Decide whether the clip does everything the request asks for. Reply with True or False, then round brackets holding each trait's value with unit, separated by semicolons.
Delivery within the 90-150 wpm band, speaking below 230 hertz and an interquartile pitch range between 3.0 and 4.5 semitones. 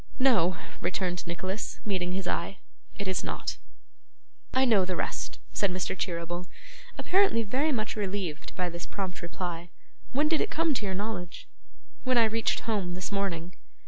False (160 wpm; 190 Hz; 4.0 semitones)